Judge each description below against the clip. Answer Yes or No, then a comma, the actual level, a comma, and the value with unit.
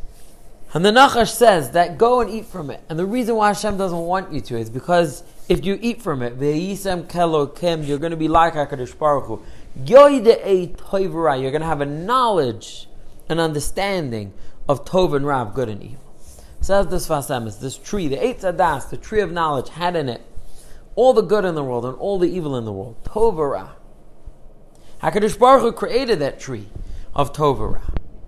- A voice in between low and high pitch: Yes, medium, 165 Hz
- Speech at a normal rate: Yes, average, 185 wpm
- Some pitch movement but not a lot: No, wide, 6.5 semitones